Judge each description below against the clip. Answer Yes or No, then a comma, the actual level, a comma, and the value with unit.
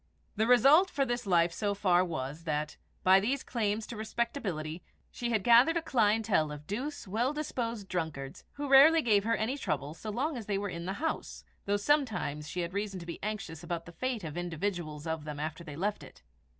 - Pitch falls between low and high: No, high, 205 Hz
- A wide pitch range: Yes, wide, 6.1 semitones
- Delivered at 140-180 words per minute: No, fast, 205 wpm